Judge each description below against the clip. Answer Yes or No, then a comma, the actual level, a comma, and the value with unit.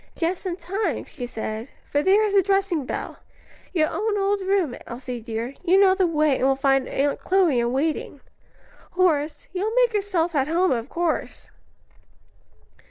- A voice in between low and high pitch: No, very high, 335 Hz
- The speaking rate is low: No, average, 170 wpm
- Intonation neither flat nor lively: No, wide, 6.2 semitones